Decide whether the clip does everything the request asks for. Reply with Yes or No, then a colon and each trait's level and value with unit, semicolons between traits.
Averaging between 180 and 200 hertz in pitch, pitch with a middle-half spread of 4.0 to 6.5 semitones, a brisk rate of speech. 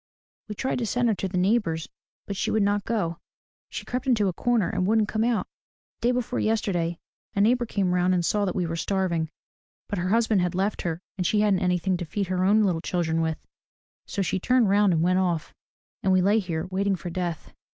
No: high, 190 Hz; average, 3.2 semitones; fast, 225 wpm